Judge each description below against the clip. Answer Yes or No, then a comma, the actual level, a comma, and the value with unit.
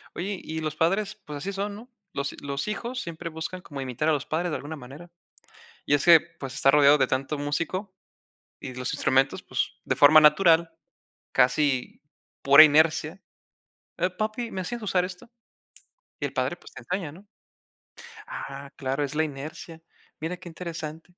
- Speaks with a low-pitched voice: No, medium, 155 Hz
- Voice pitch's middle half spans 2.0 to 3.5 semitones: No, average, 4.0 semitones